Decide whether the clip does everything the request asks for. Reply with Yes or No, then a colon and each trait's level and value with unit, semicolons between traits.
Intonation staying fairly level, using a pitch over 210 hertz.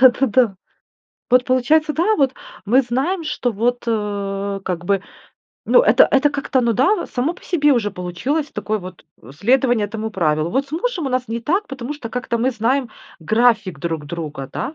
No: wide, 5.5 semitones; high, 245 Hz